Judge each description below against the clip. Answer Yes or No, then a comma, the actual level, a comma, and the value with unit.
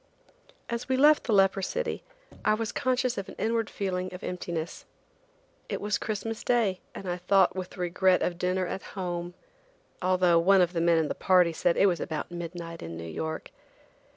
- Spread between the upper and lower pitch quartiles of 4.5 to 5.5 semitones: No, average, 3.1 semitones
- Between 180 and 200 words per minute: Yes, average, 185 wpm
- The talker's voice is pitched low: No, medium, 185 Hz